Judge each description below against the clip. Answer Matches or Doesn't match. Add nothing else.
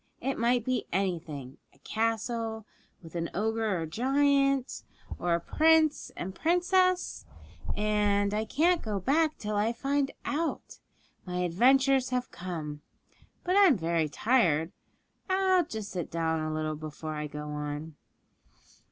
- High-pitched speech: Matches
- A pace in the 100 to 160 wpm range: Matches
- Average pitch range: Doesn't match